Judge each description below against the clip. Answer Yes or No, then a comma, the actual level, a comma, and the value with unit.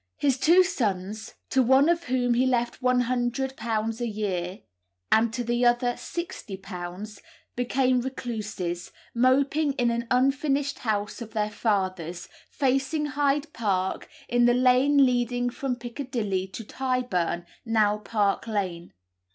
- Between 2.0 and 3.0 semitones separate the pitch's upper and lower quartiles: No, average, 3.8 semitones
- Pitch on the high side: Yes, high, 240 Hz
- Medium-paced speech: No, slow, 125 wpm